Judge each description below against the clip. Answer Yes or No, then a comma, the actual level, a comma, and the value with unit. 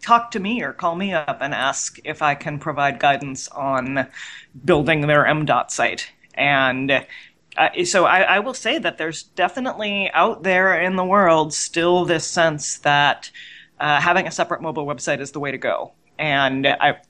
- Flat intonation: No, average, 5.1 semitones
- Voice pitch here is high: No, medium, 160 Hz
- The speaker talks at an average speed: Yes, average, 180 wpm